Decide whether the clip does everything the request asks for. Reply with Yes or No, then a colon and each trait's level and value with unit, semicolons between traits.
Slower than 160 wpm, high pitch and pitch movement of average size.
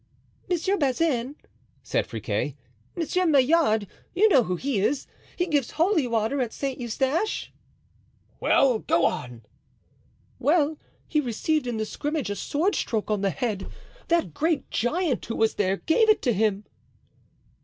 No: average, 145 wpm; very high, 270 Hz; wide, 6.6 semitones